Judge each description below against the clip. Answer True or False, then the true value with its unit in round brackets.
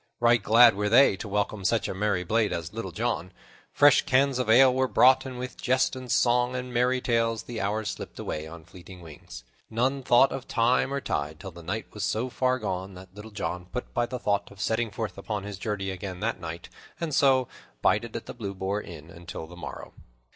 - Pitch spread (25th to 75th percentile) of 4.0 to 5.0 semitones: True (4.7 semitones)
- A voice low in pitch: True (110 Hz)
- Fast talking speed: True (220 wpm)